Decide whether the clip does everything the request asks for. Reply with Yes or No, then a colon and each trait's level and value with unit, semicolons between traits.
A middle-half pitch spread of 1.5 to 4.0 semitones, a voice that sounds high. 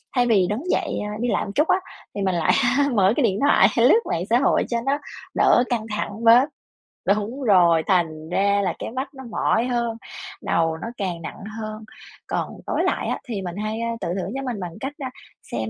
No: average, 4.7 semitones; high, 215 Hz